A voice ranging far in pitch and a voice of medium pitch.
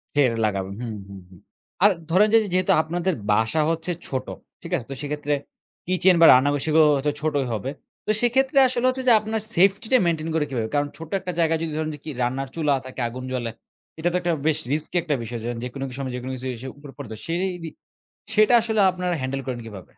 Yes: wide, 5.8 semitones; medium, 155 Hz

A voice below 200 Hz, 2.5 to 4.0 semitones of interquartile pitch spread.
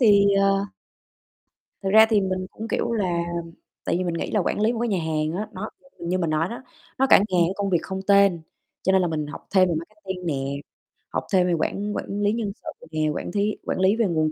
Yes: high, 190 Hz; average, 3.3 semitones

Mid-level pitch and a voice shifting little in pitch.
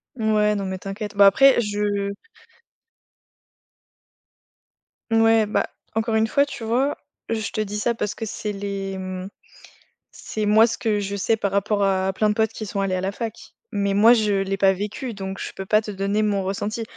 No: high, 210 Hz; narrow, 2.1 semitones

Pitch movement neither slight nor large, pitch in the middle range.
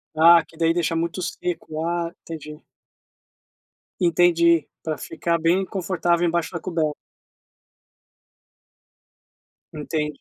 No: narrow, 1.3 semitones; medium, 170 Hz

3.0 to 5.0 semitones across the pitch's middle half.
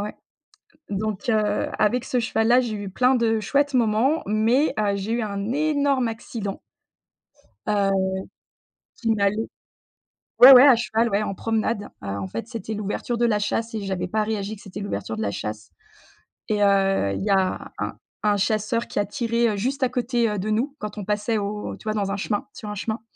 No: narrow, 2.6 semitones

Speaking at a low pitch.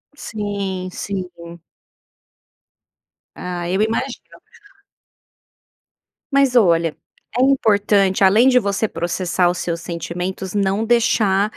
No: high, 195 Hz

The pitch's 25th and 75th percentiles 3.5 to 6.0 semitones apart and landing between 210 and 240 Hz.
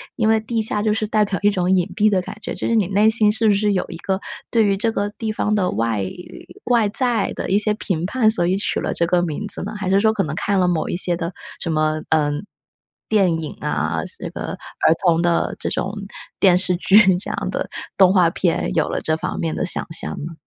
No: average, 4.0 semitones; high, 190 Hz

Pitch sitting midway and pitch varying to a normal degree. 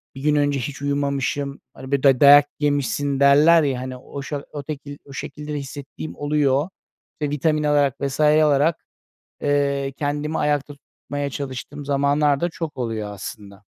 No: medium, 145 Hz; narrow, 1.3 semitones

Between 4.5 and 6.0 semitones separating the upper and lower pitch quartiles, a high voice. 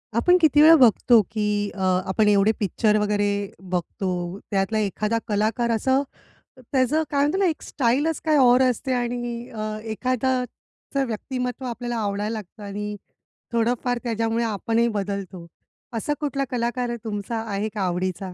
No: average, 3.5 semitones; high, 230 Hz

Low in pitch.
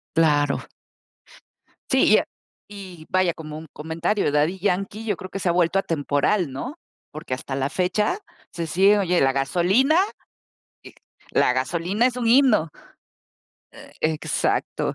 No: medium, 175 Hz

